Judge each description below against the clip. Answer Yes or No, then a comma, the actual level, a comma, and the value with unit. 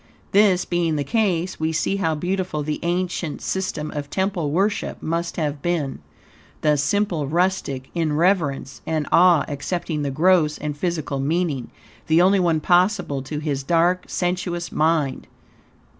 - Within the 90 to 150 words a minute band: Yes, average, 145 wpm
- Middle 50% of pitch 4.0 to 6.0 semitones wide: No, average, 3.5 semitones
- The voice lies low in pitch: No, medium, 165 Hz